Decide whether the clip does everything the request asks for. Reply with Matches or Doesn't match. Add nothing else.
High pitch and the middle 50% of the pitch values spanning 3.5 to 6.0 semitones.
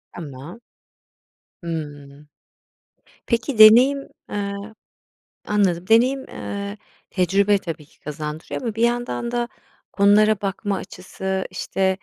Matches